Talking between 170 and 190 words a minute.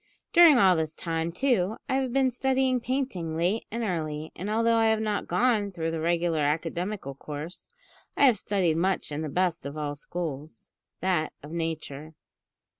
Yes: average, 175 wpm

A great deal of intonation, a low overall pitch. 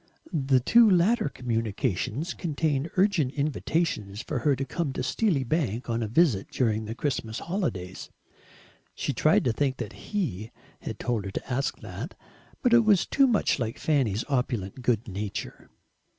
Yes: wide, 6.8 semitones; low, 130 Hz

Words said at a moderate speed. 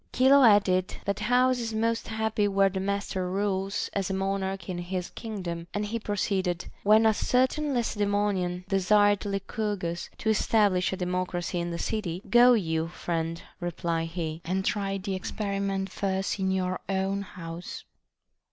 Yes: average, 150 wpm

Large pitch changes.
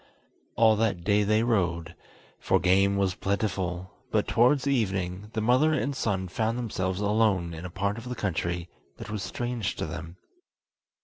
No: average, 3.9 semitones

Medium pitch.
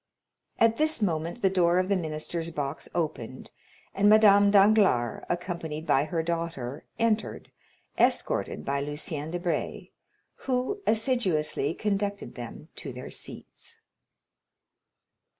Yes: medium, 175 Hz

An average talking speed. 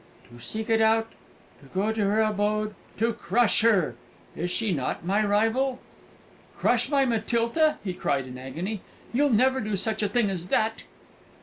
Yes: average, 170 wpm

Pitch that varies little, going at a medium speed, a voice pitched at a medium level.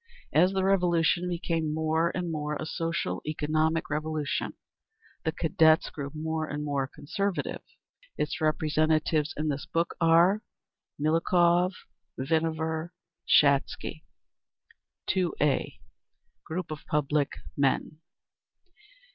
No: narrow, 2.0 semitones; slow, 100 wpm; medium, 160 Hz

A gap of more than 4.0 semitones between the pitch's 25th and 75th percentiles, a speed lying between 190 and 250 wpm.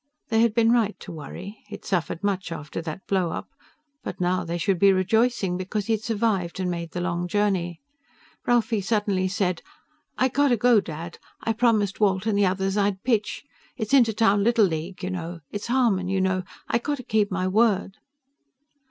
No: average, 3.5 semitones; average, 195 wpm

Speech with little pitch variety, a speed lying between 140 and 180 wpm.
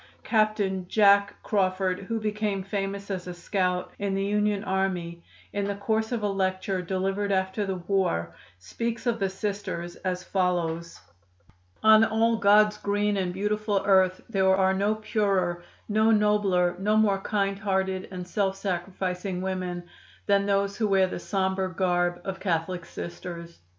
Yes: narrow, 2.0 semitones; average, 150 wpm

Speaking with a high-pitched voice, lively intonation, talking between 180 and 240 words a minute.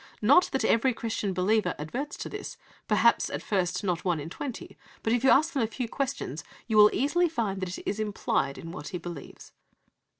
Yes: high, 215 Hz; wide, 6.0 semitones; average, 200 wpm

